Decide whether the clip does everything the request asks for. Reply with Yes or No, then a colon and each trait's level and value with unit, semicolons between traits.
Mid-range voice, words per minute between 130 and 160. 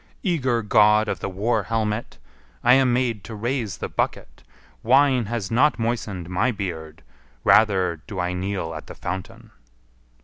No: low, 105 Hz; average, 150 wpm